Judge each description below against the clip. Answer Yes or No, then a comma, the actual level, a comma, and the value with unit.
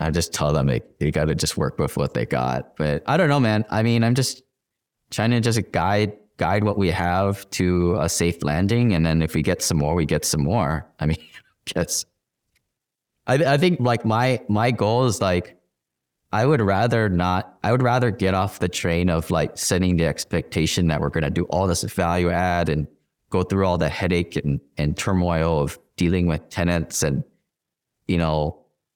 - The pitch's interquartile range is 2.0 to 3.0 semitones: No, average, 4.8 semitones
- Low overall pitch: Yes, very low, 90 Hz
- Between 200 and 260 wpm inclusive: Yes, fast, 205 wpm